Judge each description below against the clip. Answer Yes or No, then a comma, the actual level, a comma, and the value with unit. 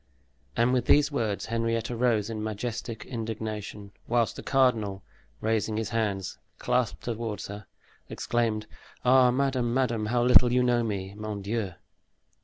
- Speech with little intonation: Yes, narrow, 2.3 semitones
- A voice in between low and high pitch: No, low, 115 Hz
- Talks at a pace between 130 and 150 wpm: Yes, average, 140 wpm